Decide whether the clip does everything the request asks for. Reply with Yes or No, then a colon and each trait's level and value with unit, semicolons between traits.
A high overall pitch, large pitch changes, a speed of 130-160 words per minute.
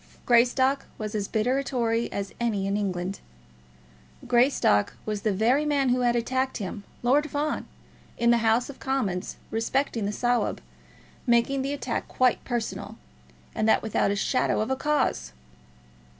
No: high, 235 Hz; average, 3.7 semitones; average, 155 wpm